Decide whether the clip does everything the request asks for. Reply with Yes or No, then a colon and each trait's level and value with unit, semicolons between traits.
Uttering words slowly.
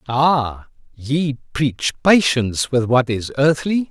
Yes: slow, 125 wpm